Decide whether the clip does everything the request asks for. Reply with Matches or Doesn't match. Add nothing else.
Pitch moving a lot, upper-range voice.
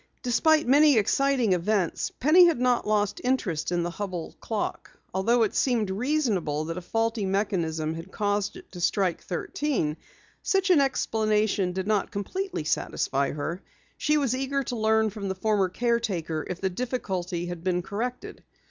Matches